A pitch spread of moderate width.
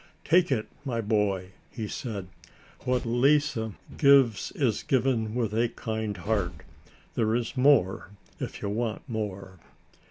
Yes: average, 3.5 semitones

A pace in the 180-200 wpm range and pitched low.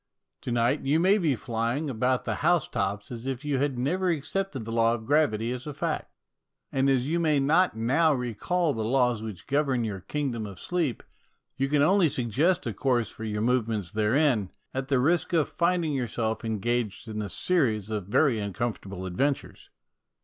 Yes: average, 185 wpm; low, 125 Hz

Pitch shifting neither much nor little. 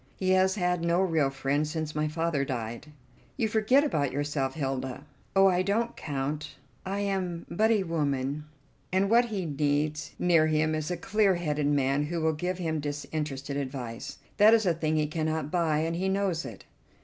Yes: average, 4.2 semitones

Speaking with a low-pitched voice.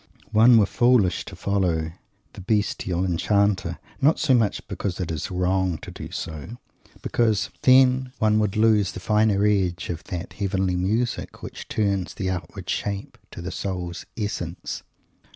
Yes: low, 100 Hz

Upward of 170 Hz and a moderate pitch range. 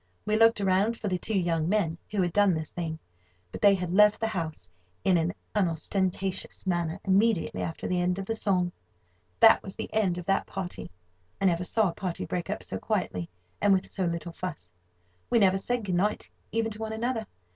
Yes: high, 190 Hz; average, 3.3 semitones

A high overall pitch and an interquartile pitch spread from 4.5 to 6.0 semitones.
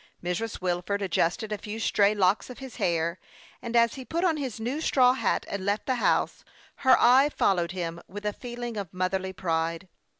Yes: high, 205 Hz; average, 4.9 semitones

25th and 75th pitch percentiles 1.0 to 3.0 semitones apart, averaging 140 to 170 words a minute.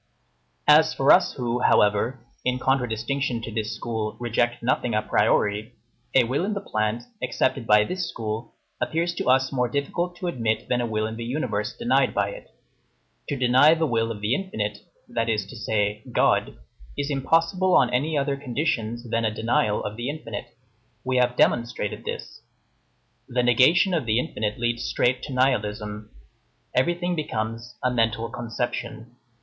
No: average, 3.8 semitones; average, 165 wpm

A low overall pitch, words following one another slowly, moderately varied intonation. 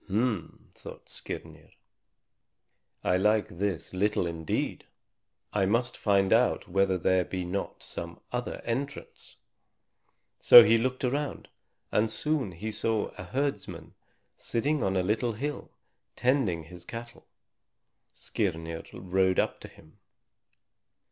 Yes: low, 105 Hz; slow, 120 wpm; average, 4.7 semitones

